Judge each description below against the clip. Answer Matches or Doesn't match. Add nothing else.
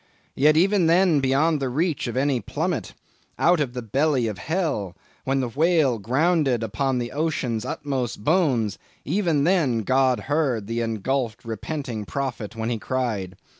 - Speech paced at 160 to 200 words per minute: Doesn't match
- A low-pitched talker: Matches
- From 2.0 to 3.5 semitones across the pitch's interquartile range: Doesn't match